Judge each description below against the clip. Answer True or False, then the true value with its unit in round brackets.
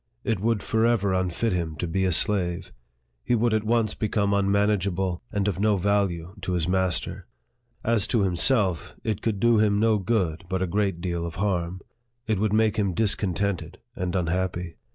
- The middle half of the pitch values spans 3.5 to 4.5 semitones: False (3.1 semitones)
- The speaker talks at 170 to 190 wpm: True (175 wpm)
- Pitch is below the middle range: True (100 Hz)